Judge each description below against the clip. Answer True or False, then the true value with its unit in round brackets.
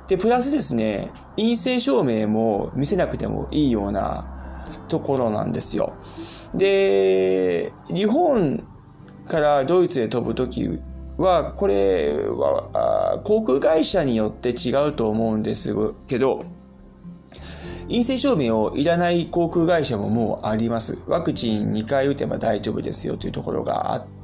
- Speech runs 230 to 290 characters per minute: True (270 characters per minute)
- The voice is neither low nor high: False (120 Hz)